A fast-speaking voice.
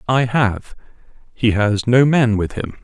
No: average, 170 wpm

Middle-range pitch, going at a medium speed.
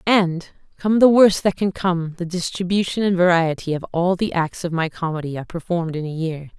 No: medium, 175 Hz; fast, 210 wpm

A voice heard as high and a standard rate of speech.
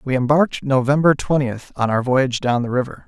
No: low, 130 Hz; average, 195 wpm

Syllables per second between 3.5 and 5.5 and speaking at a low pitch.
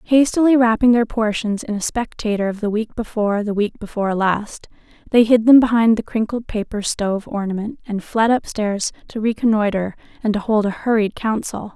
No: 5.4 syllables/s; high, 215 Hz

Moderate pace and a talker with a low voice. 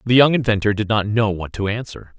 No: fast, 245 wpm; low, 105 Hz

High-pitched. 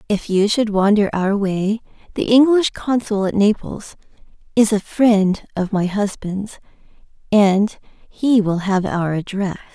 Yes: high, 205 Hz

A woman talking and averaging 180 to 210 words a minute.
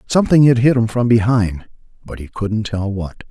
No: male; average, 200 wpm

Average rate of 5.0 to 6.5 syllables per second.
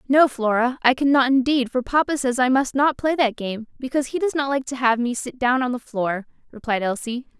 Yes: 5.5 syllables/s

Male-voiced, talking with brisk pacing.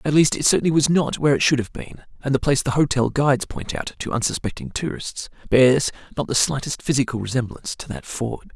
Yes: male; fast, 220 wpm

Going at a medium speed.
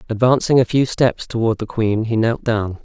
No: fast, 210 wpm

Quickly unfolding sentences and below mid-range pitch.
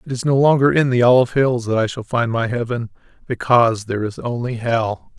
Yes: fast, 220 wpm; low, 120 Hz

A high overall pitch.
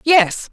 Yes: very high, 265 Hz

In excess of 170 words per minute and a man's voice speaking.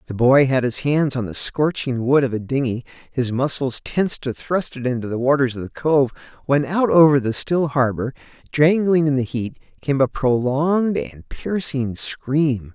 Yes: average, 190 wpm; male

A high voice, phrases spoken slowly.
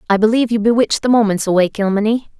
No: high, 215 Hz; average, 200 wpm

